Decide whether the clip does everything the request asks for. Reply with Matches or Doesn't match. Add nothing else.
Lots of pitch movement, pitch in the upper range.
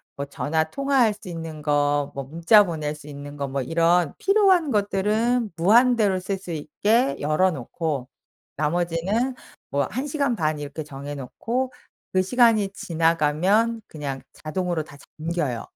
Doesn't match